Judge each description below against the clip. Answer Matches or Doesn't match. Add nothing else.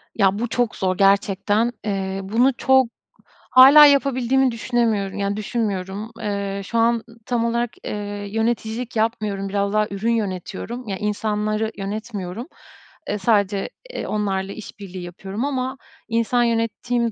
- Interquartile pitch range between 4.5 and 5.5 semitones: Doesn't match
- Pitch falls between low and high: Doesn't match